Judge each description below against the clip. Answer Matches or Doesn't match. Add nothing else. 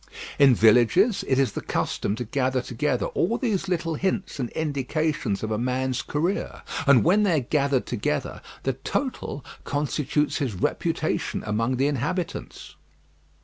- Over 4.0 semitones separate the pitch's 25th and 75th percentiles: Matches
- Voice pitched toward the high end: Doesn't match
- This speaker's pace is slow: Doesn't match